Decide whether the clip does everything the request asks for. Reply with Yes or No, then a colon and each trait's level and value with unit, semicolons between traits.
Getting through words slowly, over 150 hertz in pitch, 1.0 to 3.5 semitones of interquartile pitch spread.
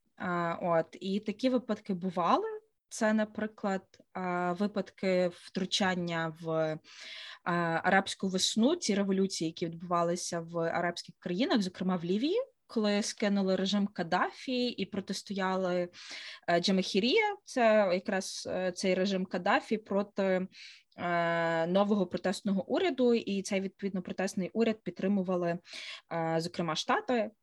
Yes: slow, 100 wpm; high, 190 Hz; average, 3.1 semitones